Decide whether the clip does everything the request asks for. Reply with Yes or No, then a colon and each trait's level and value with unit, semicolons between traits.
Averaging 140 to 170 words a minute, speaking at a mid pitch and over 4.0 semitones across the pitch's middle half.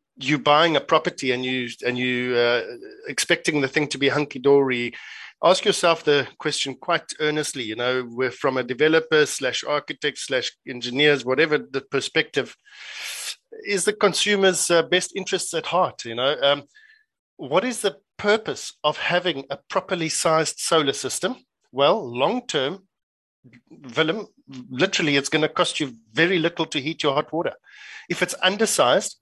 Yes: average, 150 wpm; medium, 155 Hz; average, 5.2 semitones